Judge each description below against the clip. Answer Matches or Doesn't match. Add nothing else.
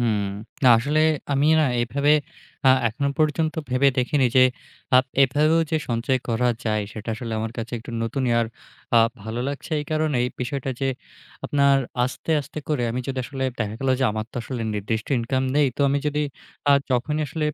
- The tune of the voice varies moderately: Matches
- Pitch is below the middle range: Matches